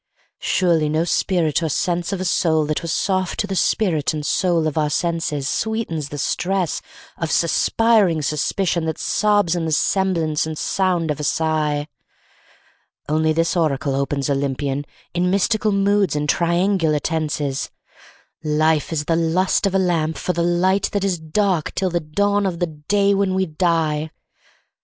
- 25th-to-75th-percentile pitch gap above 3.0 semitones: Yes, average, 3.6 semitones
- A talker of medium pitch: Yes, medium, 165 Hz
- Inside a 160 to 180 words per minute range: Yes, average, 165 wpm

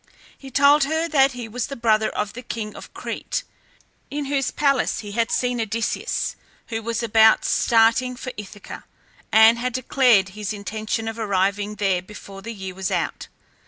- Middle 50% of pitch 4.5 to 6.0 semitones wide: No, average, 3.2 semitones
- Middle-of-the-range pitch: No, high, 225 Hz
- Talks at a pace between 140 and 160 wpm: No, average, 170 wpm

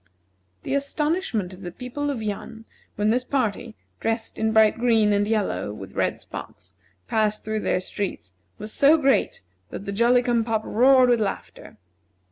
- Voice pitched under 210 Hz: No, high, 220 Hz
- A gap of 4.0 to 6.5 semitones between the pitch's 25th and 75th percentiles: No, average, 3.3 semitones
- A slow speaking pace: No, average, 165 wpm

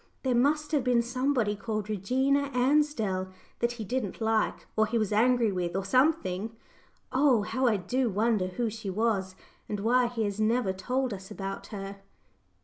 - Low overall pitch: No, high, 225 Hz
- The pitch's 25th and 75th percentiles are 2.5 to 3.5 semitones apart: No, average, 4.1 semitones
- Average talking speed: Yes, average, 170 wpm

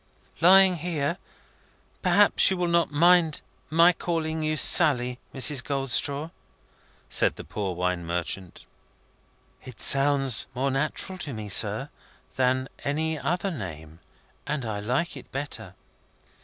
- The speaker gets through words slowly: Yes, slow, 125 wpm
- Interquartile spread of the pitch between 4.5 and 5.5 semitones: Yes, average, 5.2 semitones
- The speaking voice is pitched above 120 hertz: Yes, medium, 140 Hz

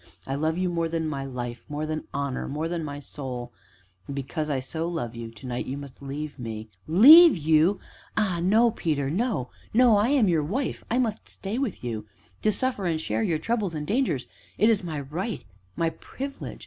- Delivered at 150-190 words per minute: No, fast, 205 wpm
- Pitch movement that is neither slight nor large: No, wide, 7.0 semitones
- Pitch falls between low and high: Yes, medium, 160 Hz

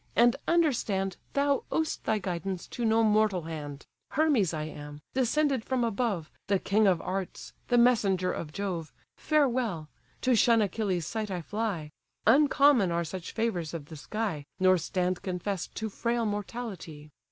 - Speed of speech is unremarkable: Yes, average, 150 wpm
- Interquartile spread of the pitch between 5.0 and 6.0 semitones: Yes, wide, 5.4 semitones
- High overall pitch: Yes, high, 200 Hz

